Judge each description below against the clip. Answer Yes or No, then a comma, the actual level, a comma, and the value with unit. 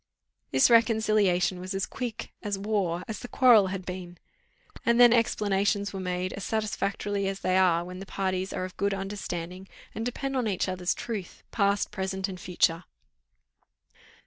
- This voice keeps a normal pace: Yes, average, 165 wpm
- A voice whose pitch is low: No, high, 195 Hz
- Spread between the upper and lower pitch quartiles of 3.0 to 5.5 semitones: No, narrow, 2.6 semitones